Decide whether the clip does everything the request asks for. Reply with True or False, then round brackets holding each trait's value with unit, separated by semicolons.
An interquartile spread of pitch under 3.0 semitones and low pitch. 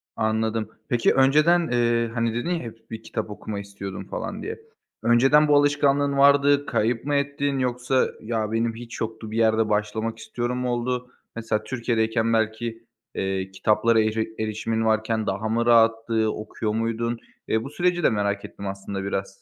True (2.4 semitones; 115 Hz)